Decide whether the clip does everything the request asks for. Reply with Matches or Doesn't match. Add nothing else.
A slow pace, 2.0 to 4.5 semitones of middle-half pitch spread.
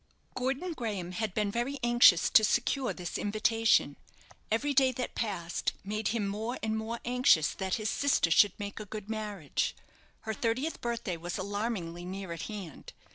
Doesn't match